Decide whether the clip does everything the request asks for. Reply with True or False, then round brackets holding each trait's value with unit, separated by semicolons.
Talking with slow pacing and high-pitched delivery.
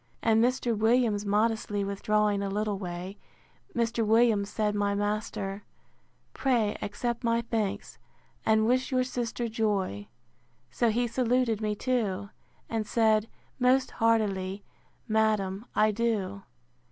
True (120 wpm; 215 Hz)